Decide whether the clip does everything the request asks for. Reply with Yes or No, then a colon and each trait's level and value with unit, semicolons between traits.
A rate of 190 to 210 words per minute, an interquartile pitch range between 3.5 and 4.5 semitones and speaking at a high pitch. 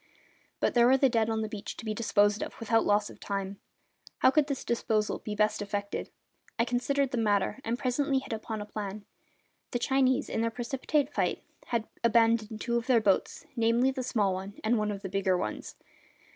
No: average, 200 wpm; average, 3.0 semitones; high, 225 Hz